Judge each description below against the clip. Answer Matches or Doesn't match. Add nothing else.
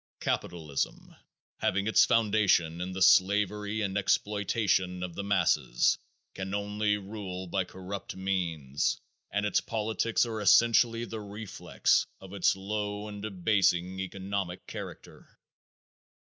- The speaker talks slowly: Matches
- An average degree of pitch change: Doesn't match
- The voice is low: Matches